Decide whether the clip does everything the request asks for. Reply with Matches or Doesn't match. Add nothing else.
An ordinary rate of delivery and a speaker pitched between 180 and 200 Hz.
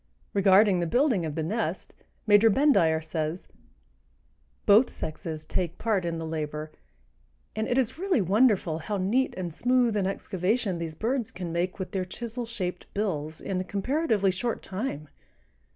Matches